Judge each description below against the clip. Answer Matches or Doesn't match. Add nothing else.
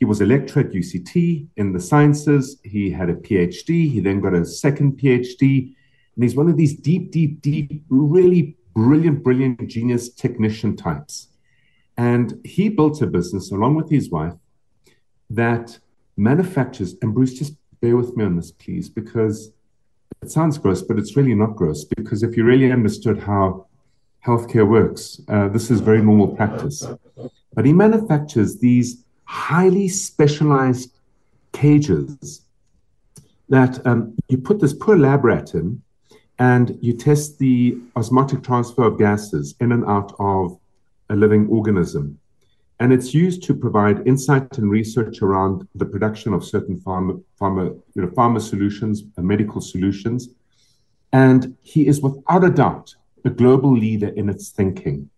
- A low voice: Matches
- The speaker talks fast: Doesn't match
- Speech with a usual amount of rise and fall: Matches